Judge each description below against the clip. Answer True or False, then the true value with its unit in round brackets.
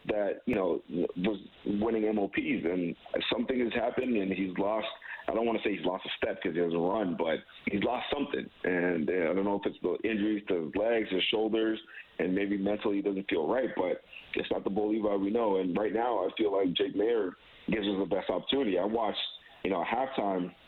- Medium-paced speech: False (230 wpm)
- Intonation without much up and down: True (2.2 semitones)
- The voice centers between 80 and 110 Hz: True (100 Hz)